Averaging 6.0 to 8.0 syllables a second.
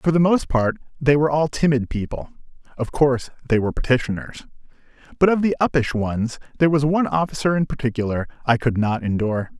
Yes: 6.3 syllables/s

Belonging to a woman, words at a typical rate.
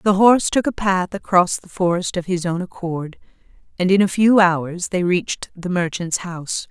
Yes: female; average, 195 wpm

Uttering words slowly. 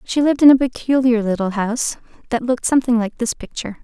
No: fast, 205 wpm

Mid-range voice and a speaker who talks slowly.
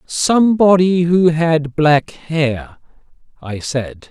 Yes: medium, 155 Hz; slow, 100 wpm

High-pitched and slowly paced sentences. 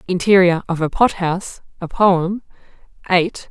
No: medium, 180 Hz; slow, 120 wpm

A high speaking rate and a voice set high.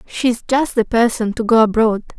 No: average, 190 wpm; high, 230 Hz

